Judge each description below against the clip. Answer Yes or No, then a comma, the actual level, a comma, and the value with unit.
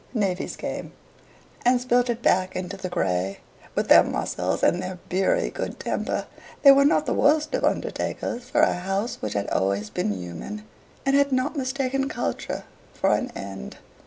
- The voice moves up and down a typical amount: No, wide, 7.4 semitones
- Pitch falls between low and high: No, high, 220 Hz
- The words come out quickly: No, average, 170 wpm